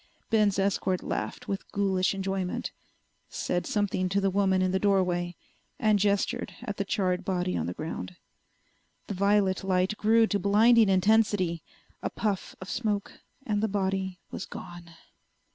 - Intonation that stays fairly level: Yes, narrow, 1.9 semitones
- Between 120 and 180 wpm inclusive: Yes, average, 150 wpm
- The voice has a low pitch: No, high, 195 Hz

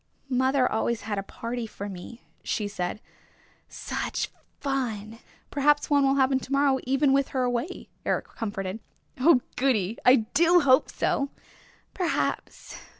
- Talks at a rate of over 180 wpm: No, average, 140 wpm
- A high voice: Yes, very high, 255 Hz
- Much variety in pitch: No, average, 3.9 semitones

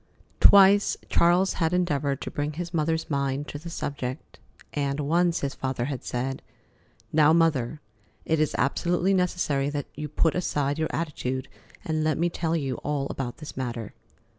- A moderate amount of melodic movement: Yes, average, 3.3 semitones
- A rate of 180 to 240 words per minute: No, average, 165 wpm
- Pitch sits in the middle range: Yes, medium, 150 Hz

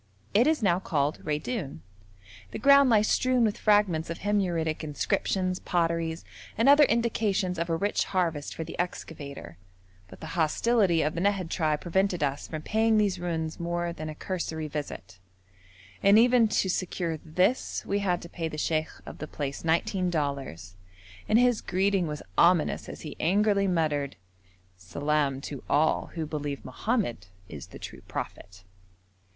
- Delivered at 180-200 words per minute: No, average, 160 wpm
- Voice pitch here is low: No, medium, 170 Hz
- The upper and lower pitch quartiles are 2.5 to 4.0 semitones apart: No, average, 4.8 semitones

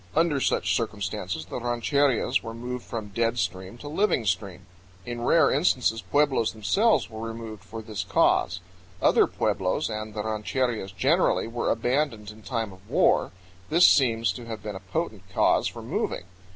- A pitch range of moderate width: Yes, average, 3.4 semitones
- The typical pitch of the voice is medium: No, low, 115 Hz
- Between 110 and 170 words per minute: Yes, average, 165 wpm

